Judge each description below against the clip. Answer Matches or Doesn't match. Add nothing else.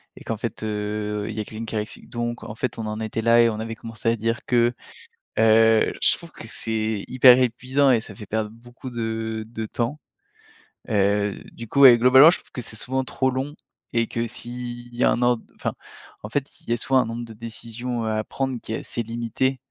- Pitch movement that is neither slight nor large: Doesn't match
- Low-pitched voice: Matches